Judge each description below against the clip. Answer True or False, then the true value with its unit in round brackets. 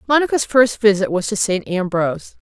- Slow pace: False (170 wpm)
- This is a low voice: False (210 Hz)